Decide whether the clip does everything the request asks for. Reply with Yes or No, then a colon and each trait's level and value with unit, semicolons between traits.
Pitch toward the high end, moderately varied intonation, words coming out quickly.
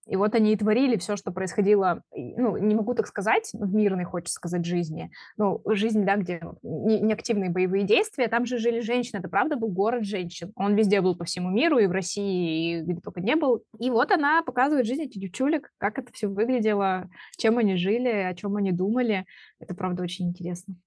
Yes: high, 205 Hz; average, 3.9 semitones; fast, 205 wpm